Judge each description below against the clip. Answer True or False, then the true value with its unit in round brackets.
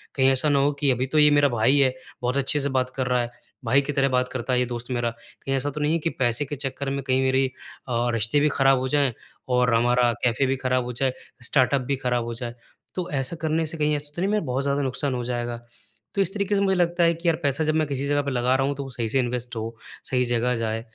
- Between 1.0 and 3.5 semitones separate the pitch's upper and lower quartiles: True (2.8 semitones)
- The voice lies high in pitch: False (135 Hz)